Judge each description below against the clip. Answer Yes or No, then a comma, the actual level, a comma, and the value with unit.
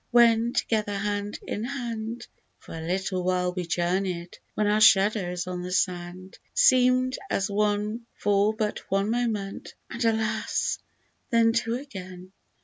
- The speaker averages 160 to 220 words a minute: No, average, 140 wpm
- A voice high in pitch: Yes, high, 205 Hz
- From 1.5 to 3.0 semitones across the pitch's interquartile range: No, average, 3.7 semitones